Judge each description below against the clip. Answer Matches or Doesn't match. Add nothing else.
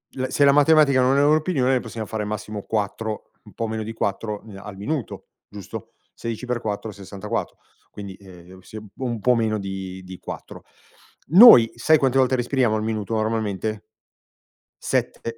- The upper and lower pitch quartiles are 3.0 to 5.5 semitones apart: Matches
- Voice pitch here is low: Matches